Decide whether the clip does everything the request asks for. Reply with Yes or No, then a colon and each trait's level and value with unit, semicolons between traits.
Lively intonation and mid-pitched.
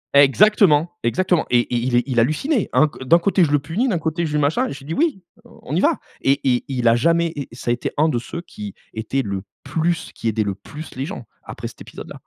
Yes: wide, 5.8 semitones; medium, 150 Hz